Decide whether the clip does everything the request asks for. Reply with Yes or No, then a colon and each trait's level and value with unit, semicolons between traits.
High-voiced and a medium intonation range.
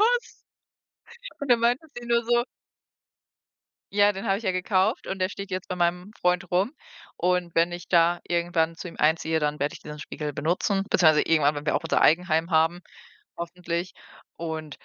No: medium, 175 Hz; average, 3.1 semitones